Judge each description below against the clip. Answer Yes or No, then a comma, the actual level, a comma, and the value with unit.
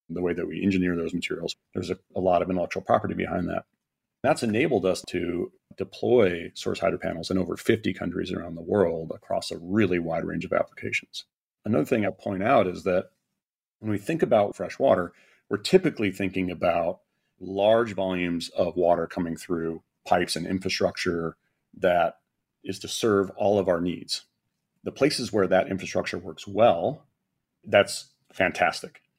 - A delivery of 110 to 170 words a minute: Yes, average, 165 wpm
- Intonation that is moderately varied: No, narrow, 2.2 semitones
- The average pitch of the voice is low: Yes, very low, 90 Hz